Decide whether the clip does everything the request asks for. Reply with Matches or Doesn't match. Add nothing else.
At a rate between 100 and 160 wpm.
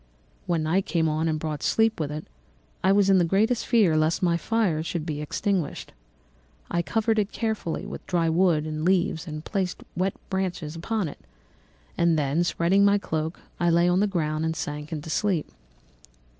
Doesn't match